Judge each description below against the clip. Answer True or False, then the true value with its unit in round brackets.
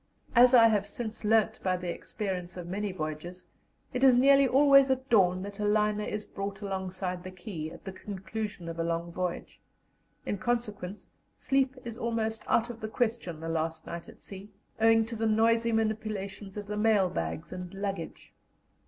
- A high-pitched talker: True (205 Hz)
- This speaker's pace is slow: False (180 wpm)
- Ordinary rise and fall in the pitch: True (3.6 semitones)